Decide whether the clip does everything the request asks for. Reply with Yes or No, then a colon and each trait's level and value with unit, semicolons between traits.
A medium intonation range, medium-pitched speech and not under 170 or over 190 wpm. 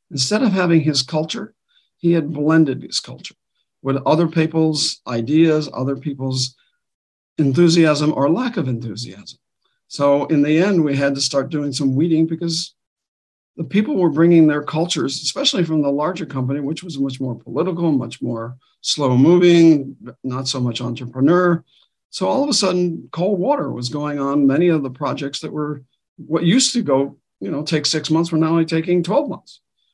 Yes: average, 3.5 semitones; medium, 155 Hz; average, 175 wpm